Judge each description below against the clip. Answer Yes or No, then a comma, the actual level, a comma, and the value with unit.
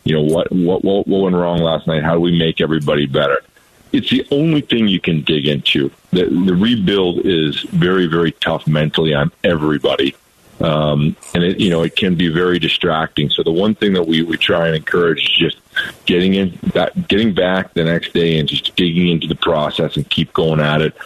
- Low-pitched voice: Yes, very low, 85 Hz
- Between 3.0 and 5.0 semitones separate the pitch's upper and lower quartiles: No, narrow, 2.6 semitones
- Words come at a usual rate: No, fast, 210 wpm